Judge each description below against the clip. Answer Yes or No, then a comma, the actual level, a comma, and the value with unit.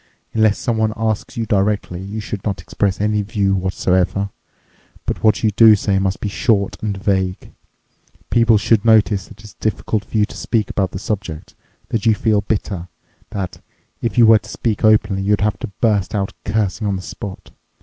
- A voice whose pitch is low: Yes, low, 105 Hz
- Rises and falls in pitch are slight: Yes, narrow, 2.0 semitones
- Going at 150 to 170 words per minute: No, average, 185 wpm